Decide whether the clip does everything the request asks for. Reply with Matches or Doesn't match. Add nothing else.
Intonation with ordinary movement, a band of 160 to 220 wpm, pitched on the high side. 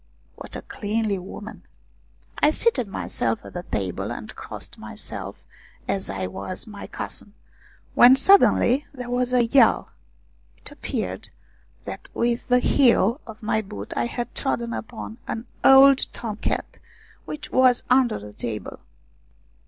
Doesn't match